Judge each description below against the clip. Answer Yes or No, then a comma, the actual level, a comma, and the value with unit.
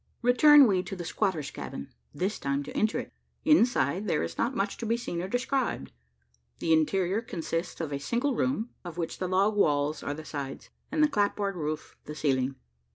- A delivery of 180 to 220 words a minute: Yes, average, 195 wpm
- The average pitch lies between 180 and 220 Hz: Yes, medium, 185 Hz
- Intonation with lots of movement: Yes, wide, 7.1 semitones